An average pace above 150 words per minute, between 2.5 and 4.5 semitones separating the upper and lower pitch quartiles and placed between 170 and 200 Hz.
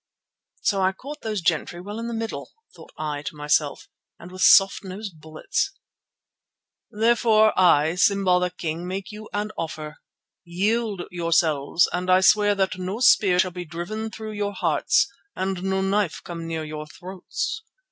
Yes: average, 160 wpm; average, 3.8 semitones; medium, 185 Hz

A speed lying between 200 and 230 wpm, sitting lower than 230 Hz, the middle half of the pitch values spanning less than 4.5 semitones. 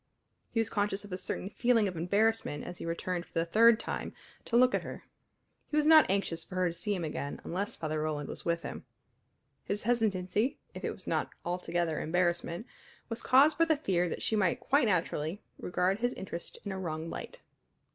No: fast, 205 wpm; high, 190 Hz; average, 4.8 semitones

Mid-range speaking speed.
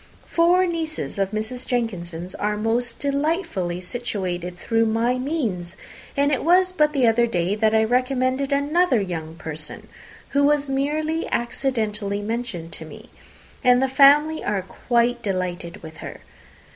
Yes: average, 145 wpm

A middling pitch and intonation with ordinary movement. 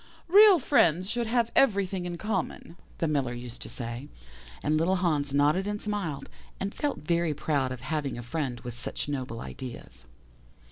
No: medium, 155 Hz; wide, 6.8 semitones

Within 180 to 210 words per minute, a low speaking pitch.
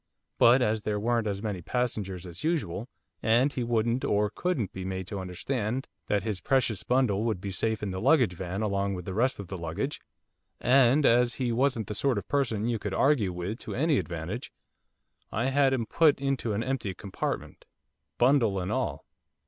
Yes: average, 190 wpm; low, 110 Hz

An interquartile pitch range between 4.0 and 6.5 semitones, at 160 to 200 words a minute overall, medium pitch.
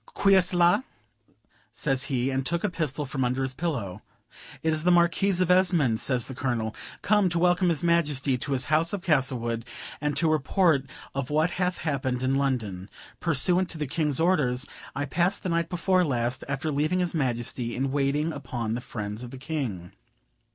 Yes: average, 5.0 semitones; average, 185 wpm; medium, 145 Hz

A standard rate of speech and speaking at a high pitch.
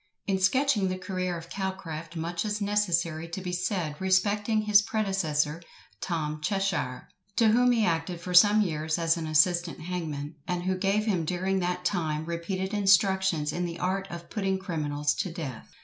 No: average, 170 wpm; medium, 180 Hz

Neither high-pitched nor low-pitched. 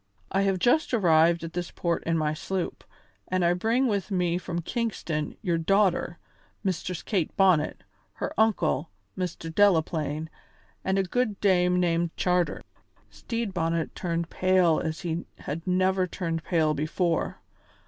Yes: medium, 175 Hz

